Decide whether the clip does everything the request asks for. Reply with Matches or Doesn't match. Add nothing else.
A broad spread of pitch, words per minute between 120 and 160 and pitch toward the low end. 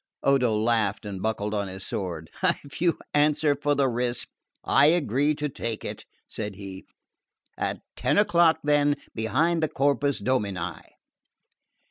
Matches